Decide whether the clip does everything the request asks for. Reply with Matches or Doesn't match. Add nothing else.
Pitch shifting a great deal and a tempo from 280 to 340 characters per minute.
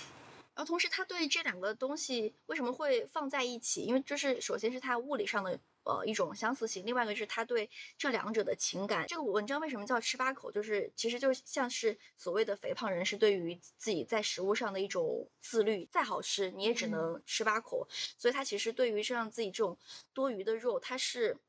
Matches